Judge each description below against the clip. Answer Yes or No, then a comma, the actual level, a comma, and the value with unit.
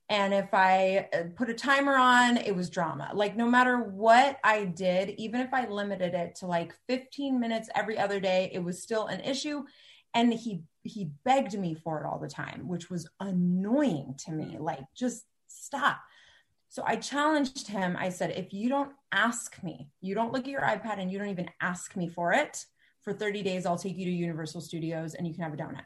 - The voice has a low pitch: No, high, 195 Hz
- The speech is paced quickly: Yes, fast, 210 wpm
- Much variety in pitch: No, average, 5.0 semitones